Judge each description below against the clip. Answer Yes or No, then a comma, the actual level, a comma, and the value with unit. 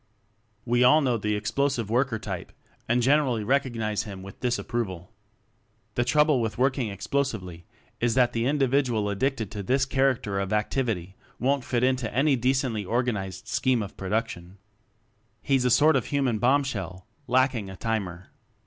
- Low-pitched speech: Yes, low, 120 Hz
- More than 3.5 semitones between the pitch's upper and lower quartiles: Yes, average, 4.2 semitones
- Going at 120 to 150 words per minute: No, average, 160 wpm